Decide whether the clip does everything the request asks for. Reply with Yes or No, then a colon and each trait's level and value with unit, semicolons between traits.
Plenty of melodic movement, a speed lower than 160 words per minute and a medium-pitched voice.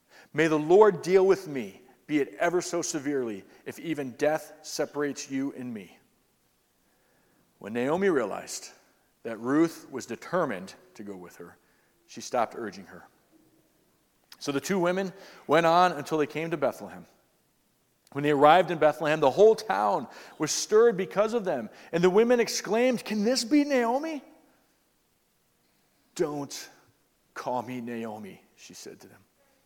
Yes: wide, 5.8 semitones; average, 150 wpm; medium, 165 Hz